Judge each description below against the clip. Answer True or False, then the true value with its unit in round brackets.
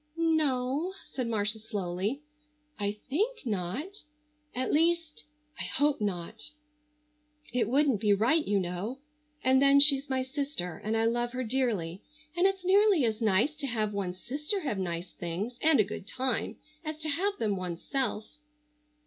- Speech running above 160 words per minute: False (155 wpm)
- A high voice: True (250 Hz)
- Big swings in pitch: True (6.4 semitones)